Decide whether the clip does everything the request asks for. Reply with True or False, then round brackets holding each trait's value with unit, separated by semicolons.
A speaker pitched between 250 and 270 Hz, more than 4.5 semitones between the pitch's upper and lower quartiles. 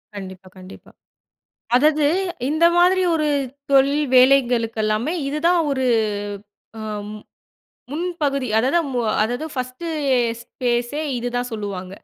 True (255 Hz; 4.9 semitones)